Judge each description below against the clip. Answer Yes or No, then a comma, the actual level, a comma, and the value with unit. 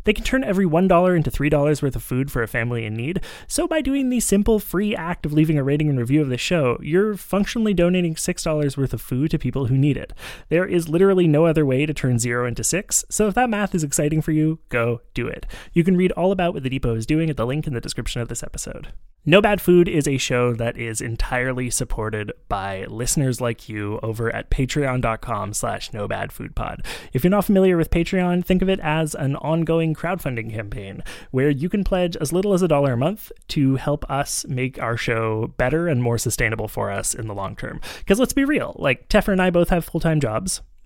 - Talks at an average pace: No, fast, 235 wpm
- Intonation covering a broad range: Yes, wide, 6.5 semitones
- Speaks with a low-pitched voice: No, medium, 150 Hz